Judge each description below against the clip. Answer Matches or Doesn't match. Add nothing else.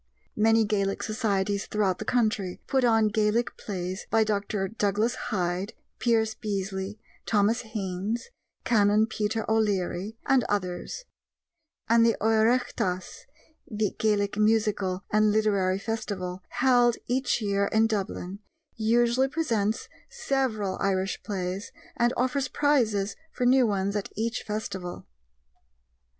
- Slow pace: Matches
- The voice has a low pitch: Doesn't match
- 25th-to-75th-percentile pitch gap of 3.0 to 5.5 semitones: Doesn't match